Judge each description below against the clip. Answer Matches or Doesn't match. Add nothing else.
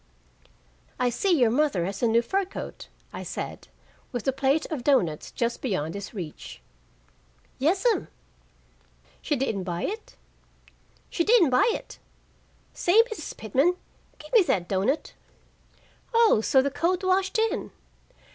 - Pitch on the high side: Matches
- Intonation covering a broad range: Matches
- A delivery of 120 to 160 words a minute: Matches